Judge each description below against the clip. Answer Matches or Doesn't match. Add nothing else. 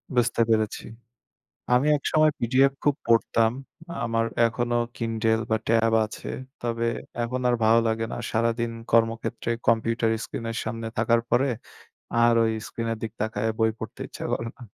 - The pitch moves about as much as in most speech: Doesn't match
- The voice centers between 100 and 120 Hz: Matches